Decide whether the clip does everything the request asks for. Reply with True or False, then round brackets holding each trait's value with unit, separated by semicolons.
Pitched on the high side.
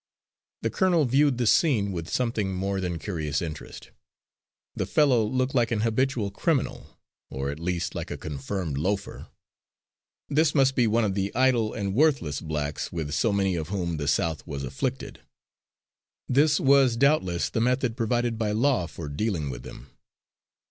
False (105 Hz)